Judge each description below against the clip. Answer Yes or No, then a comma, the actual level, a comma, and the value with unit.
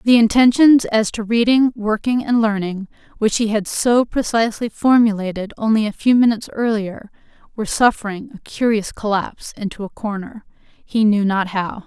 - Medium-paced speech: Yes, average, 155 wpm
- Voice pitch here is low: No, high, 220 Hz